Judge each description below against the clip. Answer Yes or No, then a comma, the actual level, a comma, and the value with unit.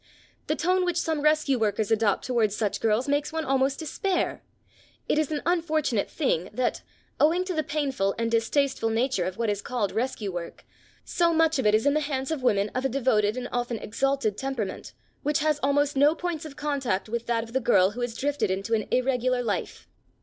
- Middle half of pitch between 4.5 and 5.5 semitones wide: Yes, average, 5.0 semitones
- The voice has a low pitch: No, very high, 260 Hz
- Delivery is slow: No, fast, 205 wpm